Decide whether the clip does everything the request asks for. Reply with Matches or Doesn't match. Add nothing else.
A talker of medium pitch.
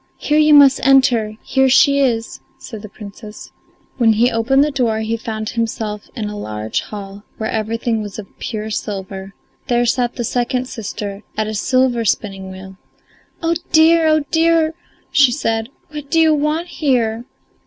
Doesn't match